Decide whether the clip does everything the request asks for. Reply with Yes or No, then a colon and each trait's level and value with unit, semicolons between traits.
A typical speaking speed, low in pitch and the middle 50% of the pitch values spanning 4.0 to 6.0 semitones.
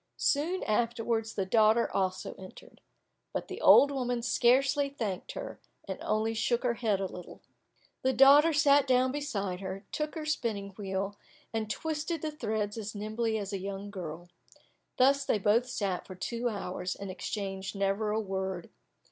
No: average, 165 wpm; high, 220 Hz; average, 4.9 semitones